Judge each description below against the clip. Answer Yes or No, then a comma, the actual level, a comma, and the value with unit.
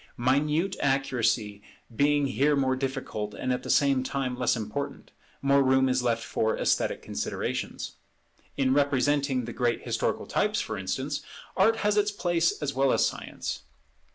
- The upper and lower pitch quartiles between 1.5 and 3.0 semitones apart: Yes, narrow, 2.4 semitones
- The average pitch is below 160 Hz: Yes, low, 135 Hz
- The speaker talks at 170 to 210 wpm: No, average, 155 wpm